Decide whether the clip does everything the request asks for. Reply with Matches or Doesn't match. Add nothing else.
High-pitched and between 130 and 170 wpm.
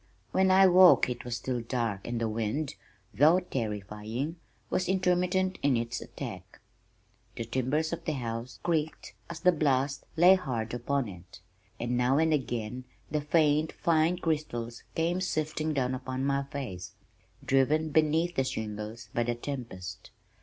Doesn't match